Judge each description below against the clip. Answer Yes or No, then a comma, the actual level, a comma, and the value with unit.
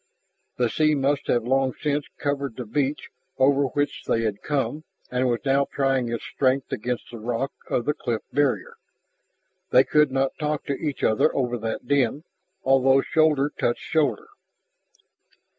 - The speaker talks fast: No, average, 160 wpm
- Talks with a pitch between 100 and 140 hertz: Yes, low, 135 Hz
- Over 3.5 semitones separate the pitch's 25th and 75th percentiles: No, average, 2.7 semitones